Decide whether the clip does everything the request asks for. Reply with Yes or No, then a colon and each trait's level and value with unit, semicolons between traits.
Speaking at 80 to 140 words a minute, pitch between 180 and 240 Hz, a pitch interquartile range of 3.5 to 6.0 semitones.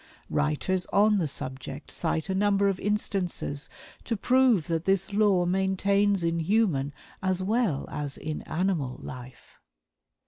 Yes: slow, 135 wpm; medium, 185 Hz; average, 4.7 semitones